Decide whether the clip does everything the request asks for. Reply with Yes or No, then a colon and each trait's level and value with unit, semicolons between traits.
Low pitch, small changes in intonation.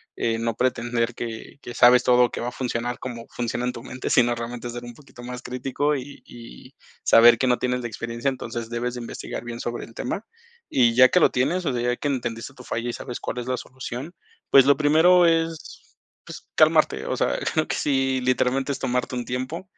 Yes: low, 125 Hz; narrow, 1.9 semitones